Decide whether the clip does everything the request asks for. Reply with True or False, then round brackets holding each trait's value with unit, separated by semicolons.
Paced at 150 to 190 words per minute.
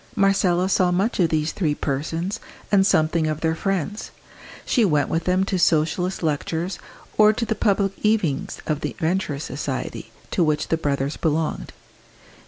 True (160 wpm)